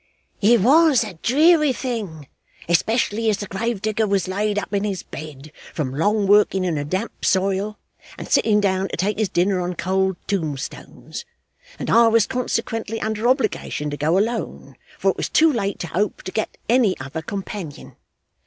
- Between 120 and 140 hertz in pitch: No, high, 205 Hz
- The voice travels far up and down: No, average, 3.6 semitones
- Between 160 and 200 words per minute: Yes, average, 175 wpm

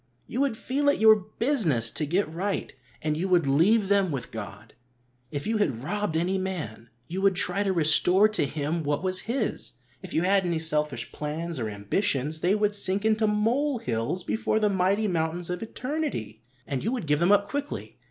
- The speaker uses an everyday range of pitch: No, wide, 5.7 semitones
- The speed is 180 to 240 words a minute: Yes, average, 195 wpm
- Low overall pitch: No, medium, 185 Hz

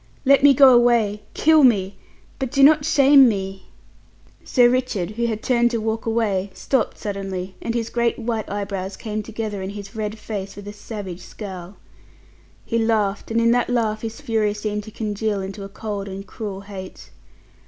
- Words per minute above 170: Yes, average, 180 wpm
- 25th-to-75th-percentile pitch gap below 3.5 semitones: Yes, average, 2.9 semitones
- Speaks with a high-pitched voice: Yes, high, 215 Hz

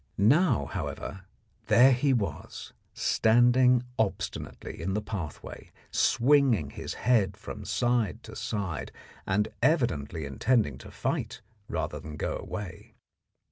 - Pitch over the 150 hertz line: No, low, 105 Hz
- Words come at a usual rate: No, slow, 115 wpm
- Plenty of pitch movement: Yes, wide, 5.7 semitones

